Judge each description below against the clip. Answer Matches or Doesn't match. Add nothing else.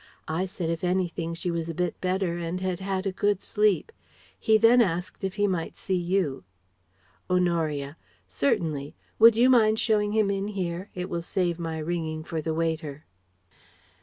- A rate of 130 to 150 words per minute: Doesn't match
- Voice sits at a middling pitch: Matches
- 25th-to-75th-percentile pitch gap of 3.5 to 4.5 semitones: Doesn't match